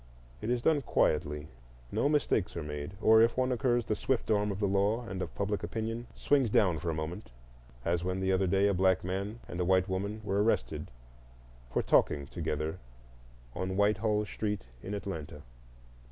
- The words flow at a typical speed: Yes, average, 180 wpm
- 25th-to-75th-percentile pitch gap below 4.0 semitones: Yes, average, 3.6 semitones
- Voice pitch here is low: Yes, low, 100 Hz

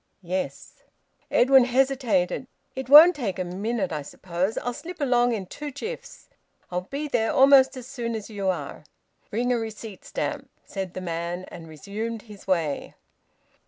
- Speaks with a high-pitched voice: Yes, high, 225 Hz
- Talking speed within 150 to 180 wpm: Yes, average, 160 wpm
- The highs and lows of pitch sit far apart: Yes, wide, 5.9 semitones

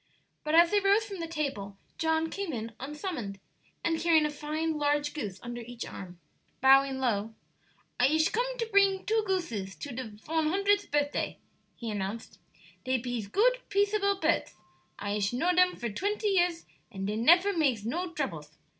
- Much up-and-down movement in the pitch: Yes, wide, 7.7 semitones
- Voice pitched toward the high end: Yes, very high, 300 Hz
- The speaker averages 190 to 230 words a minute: No, average, 170 wpm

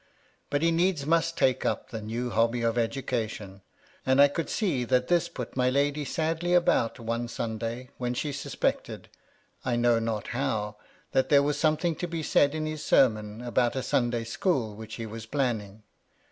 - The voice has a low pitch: Yes, low, 125 Hz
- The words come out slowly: No, average, 180 wpm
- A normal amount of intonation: Yes, average, 4.5 semitones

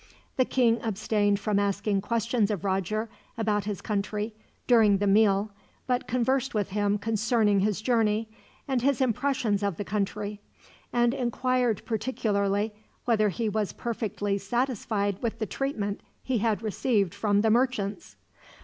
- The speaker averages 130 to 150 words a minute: Yes, average, 140 wpm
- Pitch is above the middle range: Yes, high, 215 Hz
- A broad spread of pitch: No, average, 2.7 semitones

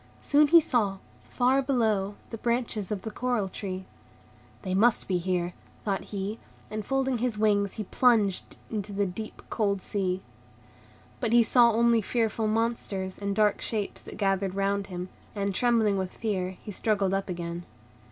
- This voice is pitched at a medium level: No, high, 205 Hz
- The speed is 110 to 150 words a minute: No, average, 160 wpm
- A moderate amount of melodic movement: Yes, average, 3.1 semitones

